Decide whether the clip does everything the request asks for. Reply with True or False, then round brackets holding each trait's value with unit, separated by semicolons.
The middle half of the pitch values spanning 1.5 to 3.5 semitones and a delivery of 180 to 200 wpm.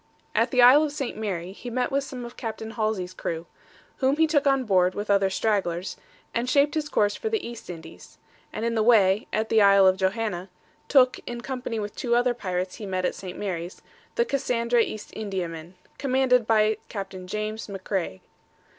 False (4.6 semitones; 190 wpm)